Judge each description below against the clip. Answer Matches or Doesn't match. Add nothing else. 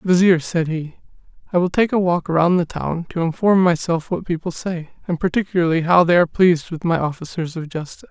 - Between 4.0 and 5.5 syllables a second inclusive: Doesn't match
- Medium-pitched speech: Matches